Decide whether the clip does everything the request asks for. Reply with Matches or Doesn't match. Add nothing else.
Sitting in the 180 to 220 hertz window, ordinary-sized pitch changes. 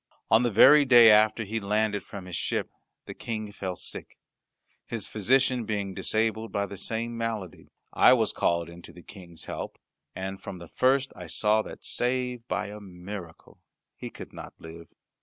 Doesn't match